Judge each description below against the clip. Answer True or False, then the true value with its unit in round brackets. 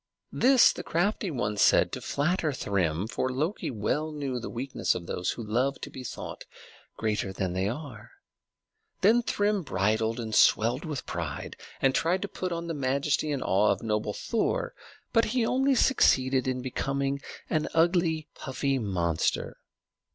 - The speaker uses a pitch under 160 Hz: True (135 Hz)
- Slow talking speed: False (160 wpm)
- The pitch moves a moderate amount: False (7.4 semitones)